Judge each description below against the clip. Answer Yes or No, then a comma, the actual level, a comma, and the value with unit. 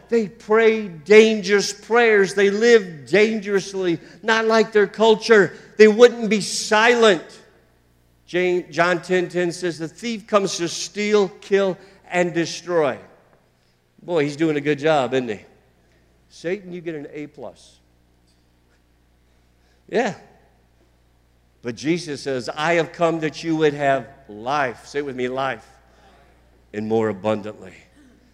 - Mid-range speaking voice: Yes, medium, 165 Hz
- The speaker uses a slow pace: Yes, slow, 130 wpm